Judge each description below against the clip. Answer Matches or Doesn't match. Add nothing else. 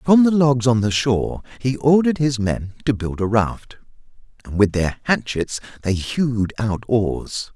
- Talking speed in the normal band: Matches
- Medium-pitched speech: Doesn't match